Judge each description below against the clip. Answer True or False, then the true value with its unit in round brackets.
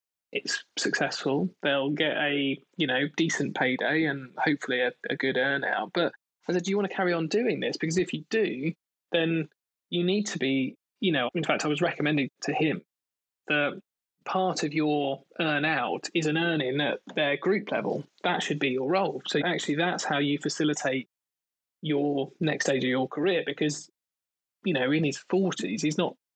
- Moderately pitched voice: True (150 Hz)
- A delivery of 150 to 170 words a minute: False (190 wpm)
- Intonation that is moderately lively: True (3.7 semitones)